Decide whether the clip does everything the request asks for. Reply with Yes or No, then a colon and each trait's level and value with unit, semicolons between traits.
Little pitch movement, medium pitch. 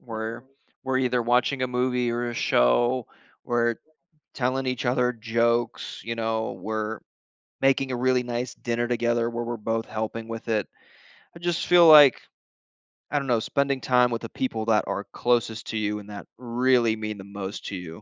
No: narrow, 2.1 semitones; low, 120 Hz